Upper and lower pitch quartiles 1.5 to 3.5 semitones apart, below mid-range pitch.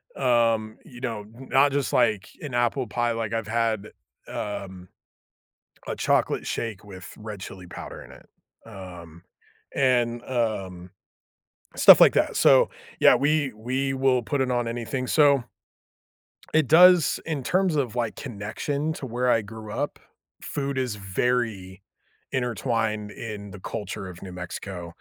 No: average, 4.3 semitones; low, 115 Hz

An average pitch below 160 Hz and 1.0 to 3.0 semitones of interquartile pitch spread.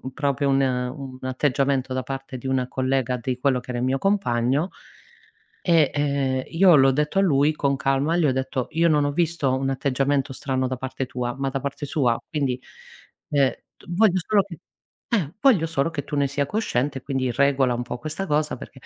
Yes: medium, 140 Hz; narrow, 2.6 semitones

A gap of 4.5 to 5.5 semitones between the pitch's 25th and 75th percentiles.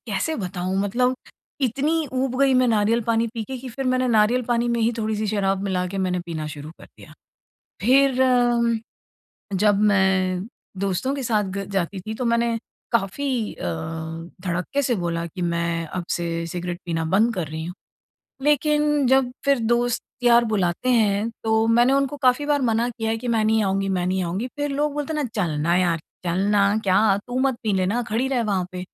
Yes: average, 5.2 semitones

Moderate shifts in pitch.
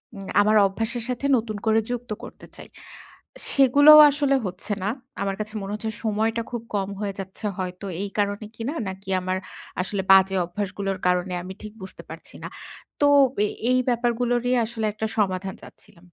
Yes: average, 3.4 semitones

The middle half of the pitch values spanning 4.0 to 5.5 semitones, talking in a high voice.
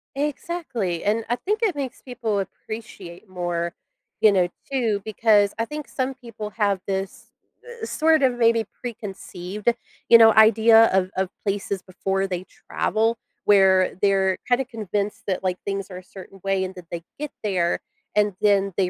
No: average, 3.4 semitones; high, 205 Hz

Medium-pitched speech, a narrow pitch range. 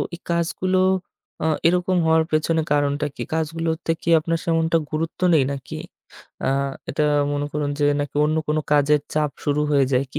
Yes: medium, 155 Hz; narrow, 2.2 semitones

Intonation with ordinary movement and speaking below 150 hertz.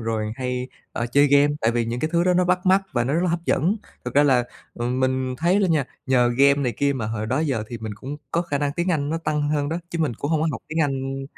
Yes: average, 4.4 semitones; medium, 140 Hz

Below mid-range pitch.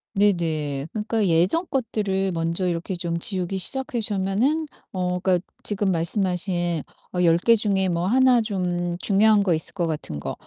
No: medium, 185 Hz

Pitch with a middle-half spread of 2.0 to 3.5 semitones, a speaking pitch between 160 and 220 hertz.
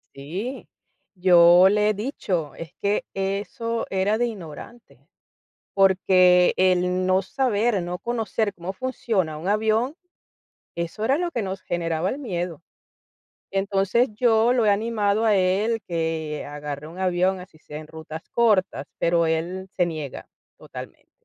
No: average, 4.3 semitones; high, 190 Hz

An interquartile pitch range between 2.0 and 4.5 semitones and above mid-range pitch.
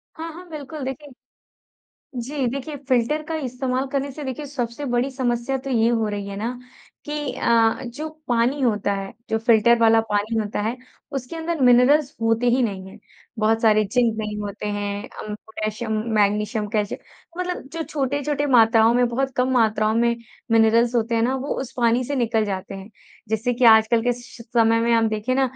Yes: average, 3.3 semitones; high, 235 Hz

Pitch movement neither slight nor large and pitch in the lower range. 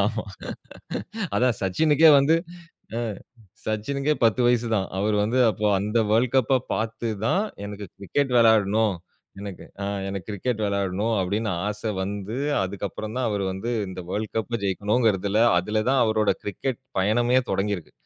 Yes: average, 3.1 semitones; low, 110 Hz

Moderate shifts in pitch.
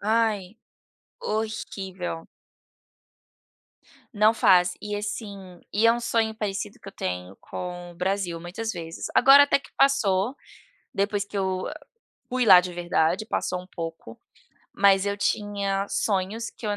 Yes: average, 3.3 semitones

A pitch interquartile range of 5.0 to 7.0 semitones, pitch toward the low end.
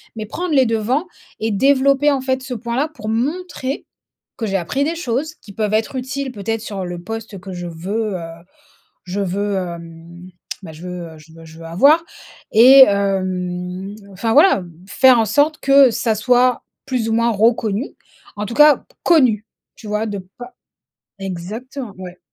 No: wide, 5.6 semitones; high, 220 Hz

